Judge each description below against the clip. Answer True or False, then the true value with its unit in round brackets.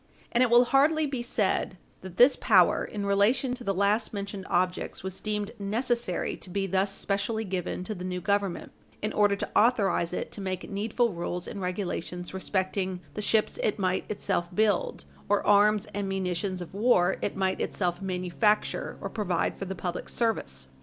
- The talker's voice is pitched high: True (200 Hz)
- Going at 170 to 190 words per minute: True (180 wpm)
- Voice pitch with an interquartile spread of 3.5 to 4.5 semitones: False (2.5 semitones)